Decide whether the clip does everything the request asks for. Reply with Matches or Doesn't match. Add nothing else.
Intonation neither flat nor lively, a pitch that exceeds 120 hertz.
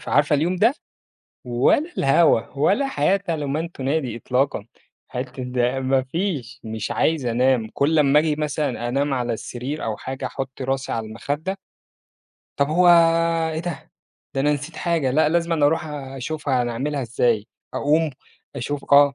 Matches